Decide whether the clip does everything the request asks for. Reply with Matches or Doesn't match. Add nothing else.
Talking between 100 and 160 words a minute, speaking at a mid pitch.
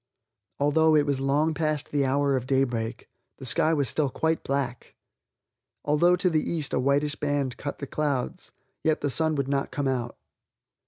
Doesn't match